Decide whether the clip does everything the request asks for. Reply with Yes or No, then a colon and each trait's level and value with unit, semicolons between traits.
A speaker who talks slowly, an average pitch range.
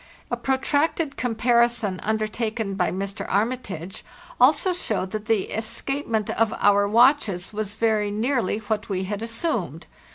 Yes: slow, 130 wpm; average, 3.1 semitones